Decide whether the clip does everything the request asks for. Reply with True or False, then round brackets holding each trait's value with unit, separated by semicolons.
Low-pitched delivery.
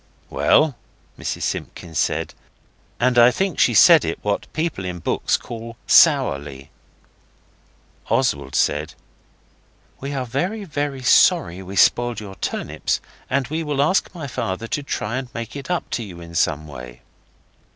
True (115 Hz)